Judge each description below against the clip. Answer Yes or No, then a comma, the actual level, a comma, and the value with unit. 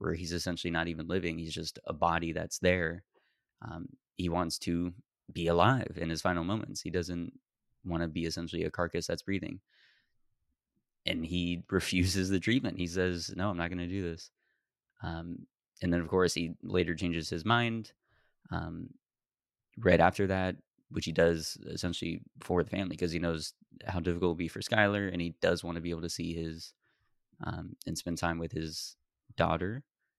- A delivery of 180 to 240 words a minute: Yes, average, 185 wpm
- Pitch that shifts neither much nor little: No, narrow, 1.8 semitones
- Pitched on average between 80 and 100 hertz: Yes, very low, 85 Hz